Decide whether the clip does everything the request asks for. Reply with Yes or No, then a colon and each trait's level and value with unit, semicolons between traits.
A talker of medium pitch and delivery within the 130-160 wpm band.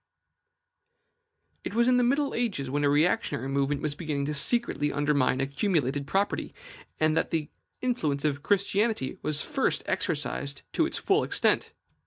Yes: medium, 150 Hz; average, 145 wpm